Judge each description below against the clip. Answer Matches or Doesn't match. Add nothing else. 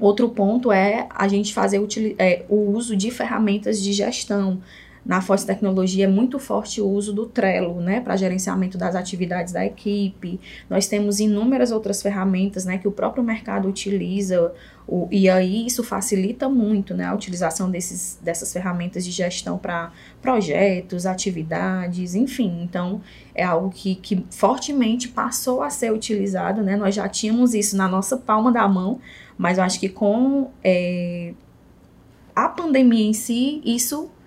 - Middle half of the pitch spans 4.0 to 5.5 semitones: Doesn't match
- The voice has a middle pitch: Doesn't match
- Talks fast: Doesn't match